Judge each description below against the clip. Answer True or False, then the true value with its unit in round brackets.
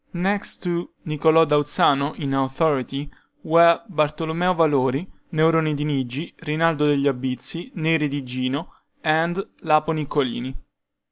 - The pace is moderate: False (120 wpm)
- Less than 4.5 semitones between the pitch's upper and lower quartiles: True (2.8 semitones)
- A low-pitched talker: False (155 Hz)